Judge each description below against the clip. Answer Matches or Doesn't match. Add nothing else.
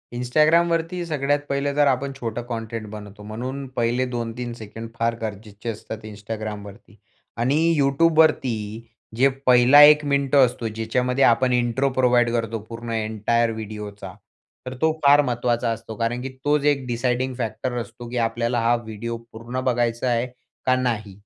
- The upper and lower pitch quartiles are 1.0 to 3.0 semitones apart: Matches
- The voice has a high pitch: Doesn't match